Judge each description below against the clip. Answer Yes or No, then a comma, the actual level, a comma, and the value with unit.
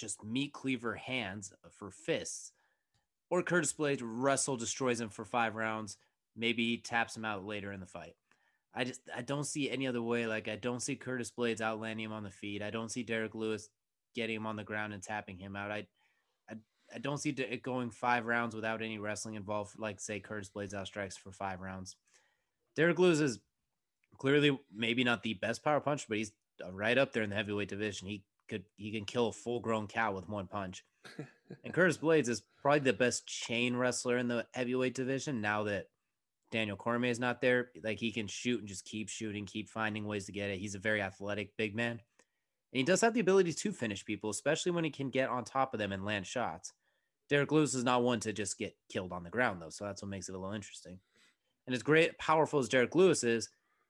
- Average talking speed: No, fast, 220 wpm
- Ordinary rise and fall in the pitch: Yes, average, 3.4 semitones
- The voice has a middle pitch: No, low, 115 Hz